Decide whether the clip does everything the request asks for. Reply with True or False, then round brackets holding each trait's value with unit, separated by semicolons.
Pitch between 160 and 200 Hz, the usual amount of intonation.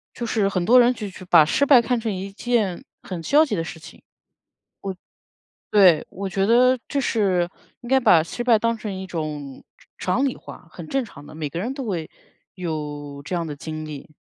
False (190 Hz; 6.7 semitones)